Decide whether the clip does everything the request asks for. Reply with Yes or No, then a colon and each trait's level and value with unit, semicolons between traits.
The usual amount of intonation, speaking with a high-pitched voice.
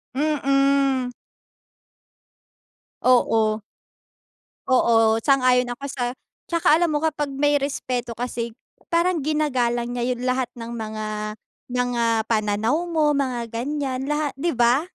Yes: average, 3.5 semitones; very high, 255 Hz